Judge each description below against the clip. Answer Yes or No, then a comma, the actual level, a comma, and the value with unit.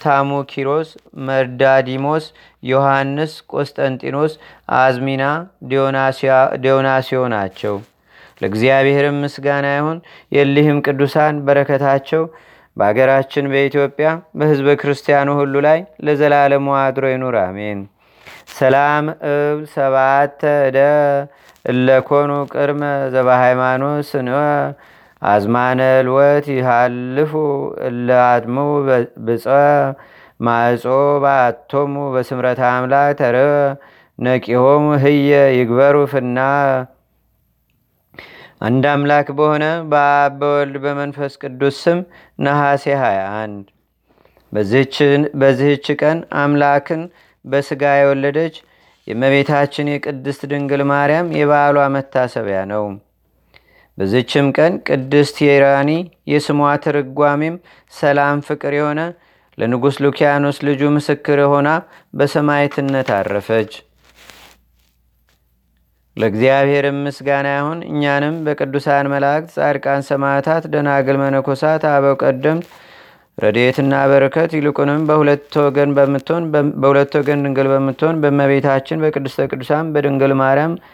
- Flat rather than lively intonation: Yes, narrow, 1.6 semitones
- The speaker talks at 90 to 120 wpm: No, average, 75 wpm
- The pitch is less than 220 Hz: Yes, medium, 140 Hz